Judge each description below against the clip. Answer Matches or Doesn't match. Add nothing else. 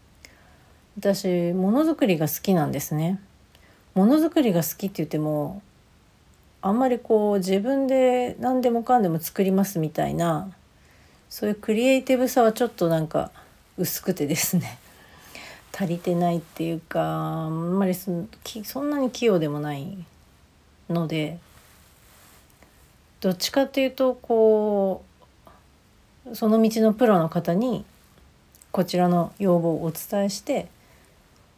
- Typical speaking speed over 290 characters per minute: Doesn't match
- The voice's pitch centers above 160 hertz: Matches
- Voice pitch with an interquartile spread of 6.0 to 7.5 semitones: Doesn't match